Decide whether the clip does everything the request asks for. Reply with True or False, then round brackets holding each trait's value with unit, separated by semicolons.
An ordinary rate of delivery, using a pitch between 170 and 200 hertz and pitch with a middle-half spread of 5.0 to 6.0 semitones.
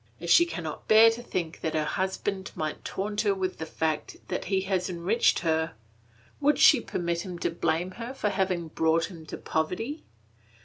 False (185 wpm; 185 Hz; 4.0 semitones)